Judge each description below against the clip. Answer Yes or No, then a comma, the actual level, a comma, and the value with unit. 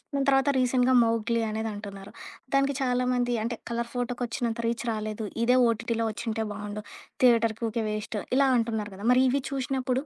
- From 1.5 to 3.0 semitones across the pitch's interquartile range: Yes, narrow, 2.4 semitones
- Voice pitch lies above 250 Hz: No, high, 235 Hz